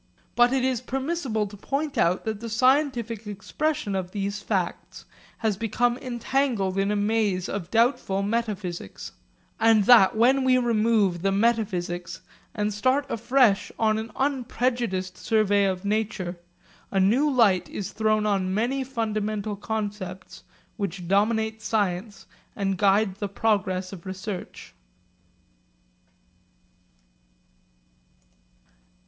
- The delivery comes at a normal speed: No, slow, 120 wpm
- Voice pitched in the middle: No, high, 215 Hz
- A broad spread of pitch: No, average, 3.3 semitones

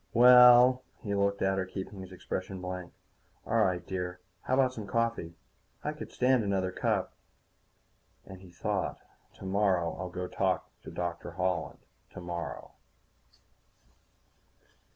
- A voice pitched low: Yes, very low, 95 Hz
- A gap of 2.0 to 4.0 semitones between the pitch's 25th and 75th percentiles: Yes, average, 3.3 semitones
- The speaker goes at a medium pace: No, slow, 130 wpm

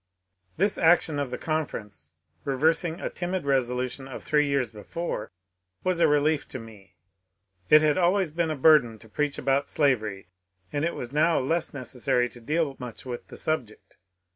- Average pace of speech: Yes, average, 170 wpm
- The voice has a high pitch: No, medium, 140 Hz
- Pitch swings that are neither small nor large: Yes, average, 4.5 semitones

